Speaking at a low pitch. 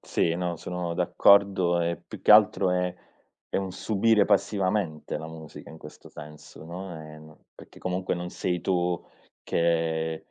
Yes: very low, 85 Hz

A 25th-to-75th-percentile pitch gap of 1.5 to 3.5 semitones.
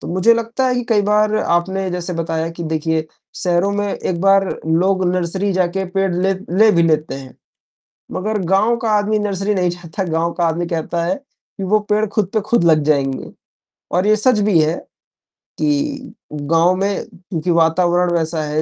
No: average, 3.9 semitones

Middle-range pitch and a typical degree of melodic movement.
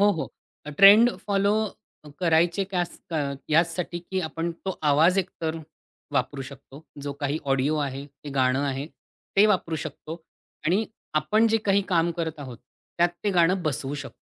Yes: medium, 165 Hz; average, 4.7 semitones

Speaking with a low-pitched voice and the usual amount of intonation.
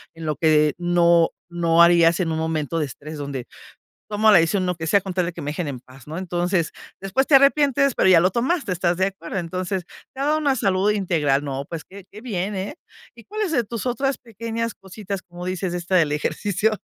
No: medium, 180 Hz; average, 4.1 semitones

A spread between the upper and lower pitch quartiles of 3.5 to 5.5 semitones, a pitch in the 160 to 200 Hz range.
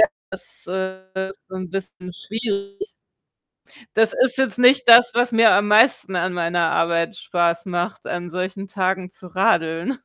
Yes: average, 3.9 semitones; high, 190 Hz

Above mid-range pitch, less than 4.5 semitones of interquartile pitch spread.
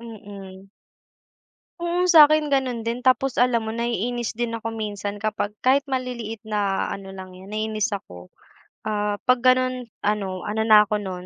Yes: high, 220 Hz; average, 3.6 semitones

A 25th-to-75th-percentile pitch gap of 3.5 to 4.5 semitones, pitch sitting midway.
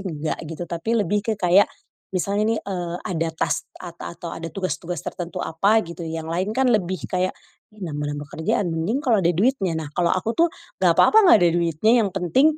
Yes: average, 4.0 semitones; medium, 180 Hz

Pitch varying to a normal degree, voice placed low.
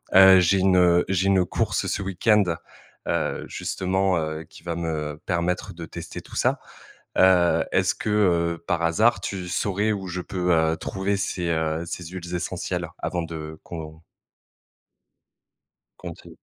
No: narrow, 2.3 semitones; very low, 90 Hz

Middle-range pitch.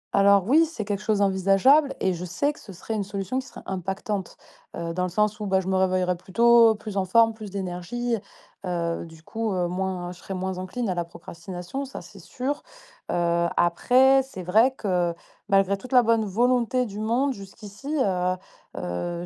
No: high, 195 Hz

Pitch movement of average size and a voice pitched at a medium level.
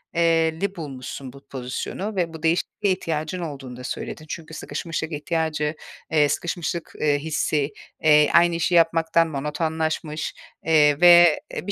No: narrow, 2.1 semitones; medium, 160 Hz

